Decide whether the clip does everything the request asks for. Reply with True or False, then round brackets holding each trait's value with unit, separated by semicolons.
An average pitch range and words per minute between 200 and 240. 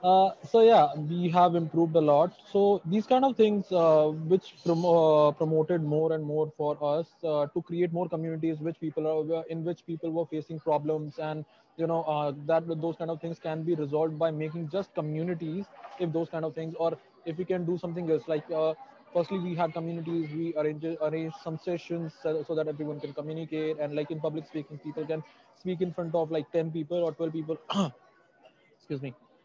False (1.8 semitones; 205 wpm)